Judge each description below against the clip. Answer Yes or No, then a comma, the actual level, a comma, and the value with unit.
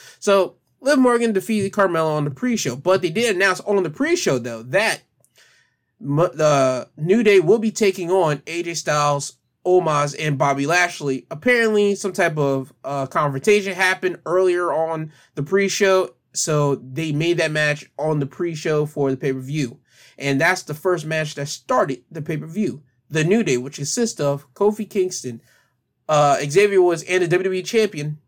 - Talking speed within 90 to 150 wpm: No, average, 165 wpm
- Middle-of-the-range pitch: Yes, medium, 160 Hz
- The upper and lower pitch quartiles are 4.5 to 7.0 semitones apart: Yes, average, 4.9 semitones